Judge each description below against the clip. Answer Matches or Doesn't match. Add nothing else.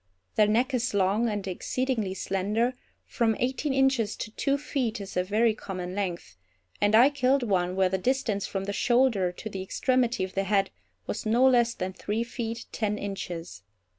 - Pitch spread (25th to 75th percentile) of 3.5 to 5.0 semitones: Matches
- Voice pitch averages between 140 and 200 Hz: Doesn't match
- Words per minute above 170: Matches